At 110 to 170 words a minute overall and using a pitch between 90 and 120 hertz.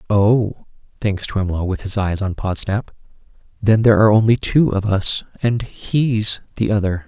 Yes: average, 160 wpm; low, 105 Hz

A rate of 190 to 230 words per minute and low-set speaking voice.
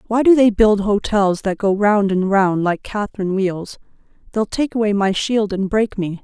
No: average, 200 wpm; high, 205 Hz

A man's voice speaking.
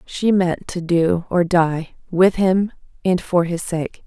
No: female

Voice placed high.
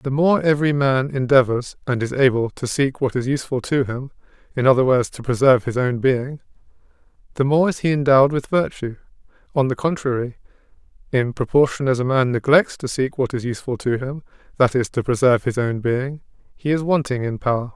No: low, 130 Hz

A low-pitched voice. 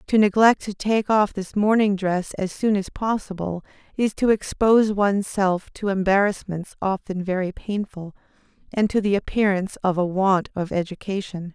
No: high, 195 Hz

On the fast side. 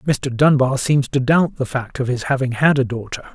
Yes: fast, 235 wpm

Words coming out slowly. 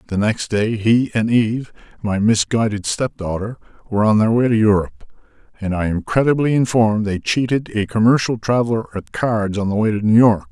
No: average, 190 wpm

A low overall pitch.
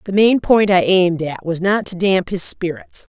No: medium, 185 Hz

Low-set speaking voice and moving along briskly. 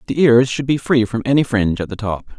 Yes: low, 120 Hz; fast, 275 wpm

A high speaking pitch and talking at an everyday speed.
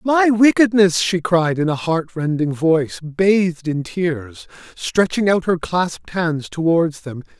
No: medium, 170 Hz; average, 145 wpm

